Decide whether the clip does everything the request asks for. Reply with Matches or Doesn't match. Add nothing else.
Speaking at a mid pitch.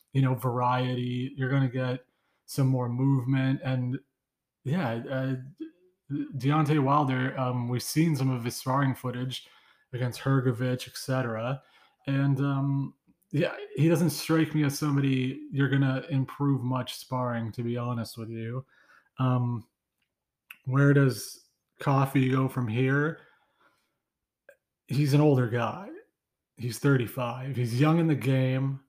Doesn't match